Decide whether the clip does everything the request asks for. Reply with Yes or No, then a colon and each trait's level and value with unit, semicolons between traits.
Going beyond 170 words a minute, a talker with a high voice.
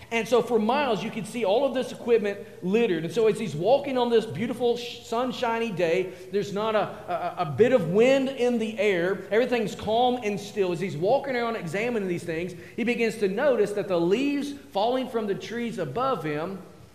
Yes: average, 200 wpm; high, 220 Hz